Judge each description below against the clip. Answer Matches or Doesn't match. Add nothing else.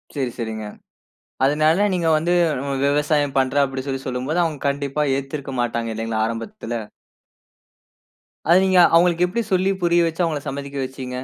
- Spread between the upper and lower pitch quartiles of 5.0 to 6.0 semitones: Doesn't match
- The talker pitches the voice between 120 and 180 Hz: Matches